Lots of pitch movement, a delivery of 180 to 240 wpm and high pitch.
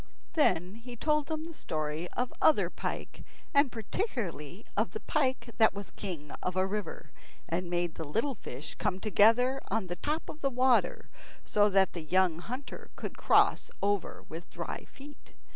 No: wide, 7.0 semitones; average, 170 wpm; high, 210 Hz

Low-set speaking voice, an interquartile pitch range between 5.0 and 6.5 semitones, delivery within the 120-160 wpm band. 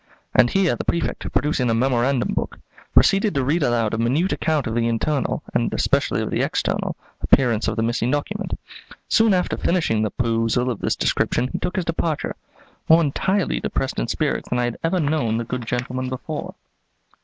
No: low, 130 Hz; wide, 5.5 semitones; average, 190 wpm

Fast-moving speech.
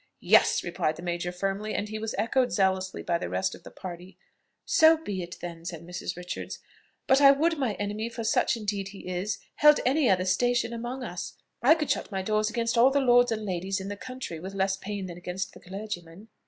Yes: fast, 220 wpm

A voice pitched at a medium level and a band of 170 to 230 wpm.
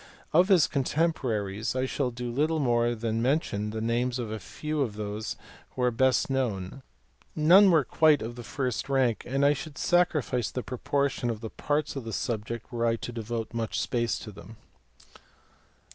No: low, 125 Hz; average, 180 wpm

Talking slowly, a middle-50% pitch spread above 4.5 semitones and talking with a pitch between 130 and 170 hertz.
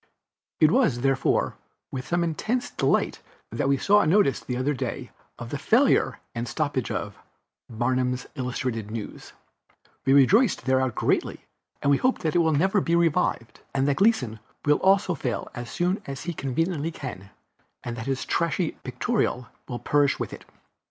No: average, 170 wpm; average, 5.3 semitones; medium, 140 Hz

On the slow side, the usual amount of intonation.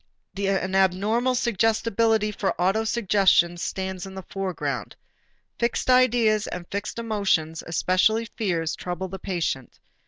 Yes: slow, 115 wpm; average, 3.3 semitones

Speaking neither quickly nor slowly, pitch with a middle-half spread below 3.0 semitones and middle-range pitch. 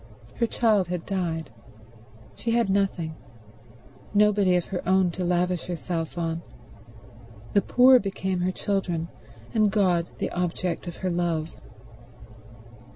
No: slow, 125 wpm; narrow, 2.6 semitones; medium, 180 Hz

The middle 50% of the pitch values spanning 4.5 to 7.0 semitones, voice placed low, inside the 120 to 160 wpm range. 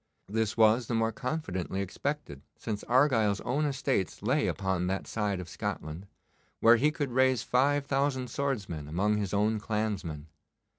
Yes: average, 5.2 semitones; low, 110 Hz; average, 150 wpm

